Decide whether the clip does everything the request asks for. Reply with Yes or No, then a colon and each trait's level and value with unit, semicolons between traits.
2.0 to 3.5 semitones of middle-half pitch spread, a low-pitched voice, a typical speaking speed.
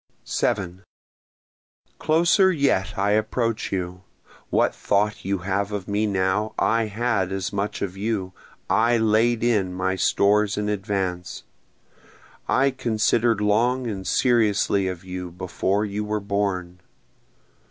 No: average, 3.0 semitones; low, 105 Hz; slow, 125 wpm